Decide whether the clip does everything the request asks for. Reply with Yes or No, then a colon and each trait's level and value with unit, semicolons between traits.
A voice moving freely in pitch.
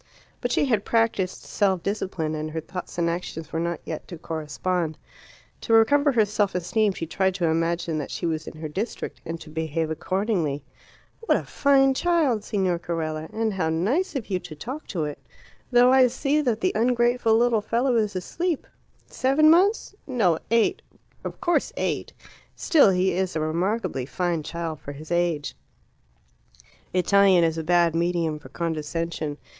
Yes: wide, 6.1 semitones